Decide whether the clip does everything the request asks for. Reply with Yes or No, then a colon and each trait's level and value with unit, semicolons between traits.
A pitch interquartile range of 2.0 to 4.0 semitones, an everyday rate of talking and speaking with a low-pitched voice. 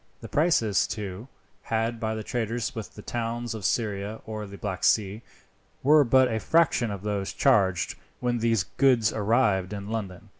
Yes: average, 2.8 semitones; average, 165 wpm; low, 110 Hz